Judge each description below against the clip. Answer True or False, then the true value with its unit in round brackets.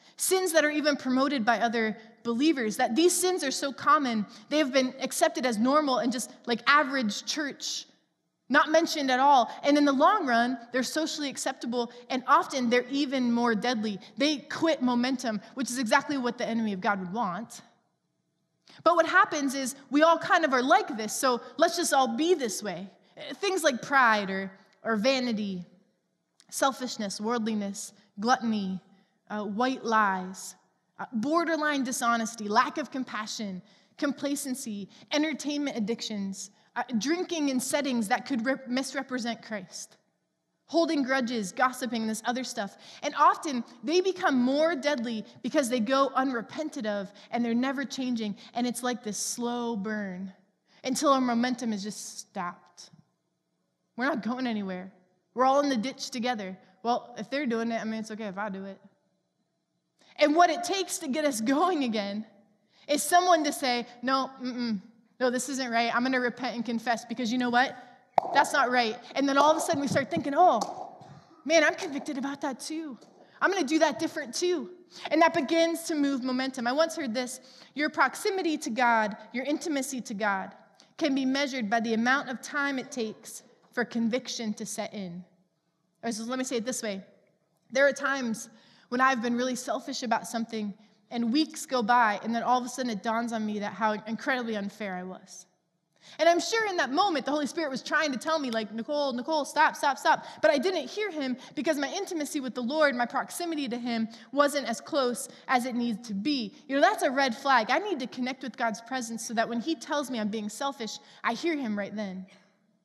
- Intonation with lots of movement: False (4.6 semitones)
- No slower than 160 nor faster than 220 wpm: True (190 wpm)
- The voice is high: True (250 Hz)